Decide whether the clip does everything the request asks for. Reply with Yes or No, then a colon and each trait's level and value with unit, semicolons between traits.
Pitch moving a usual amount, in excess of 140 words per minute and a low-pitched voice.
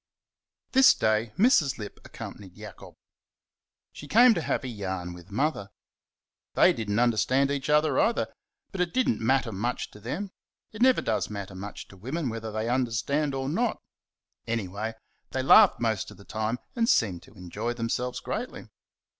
No: wide, 6.1 semitones; average, 170 wpm; low, 120 Hz